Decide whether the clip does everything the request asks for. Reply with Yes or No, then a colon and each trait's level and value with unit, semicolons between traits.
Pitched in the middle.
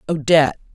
Yes: medium, 150 Hz